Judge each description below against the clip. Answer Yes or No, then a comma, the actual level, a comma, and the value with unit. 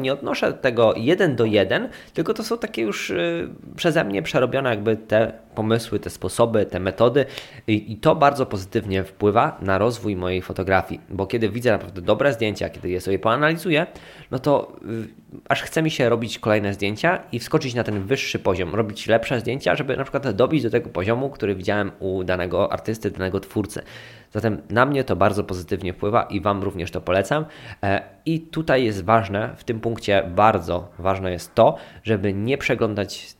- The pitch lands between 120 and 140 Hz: No, low, 110 Hz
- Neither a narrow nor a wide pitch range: Yes, average, 4.4 semitones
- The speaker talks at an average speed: No, fast, 180 wpm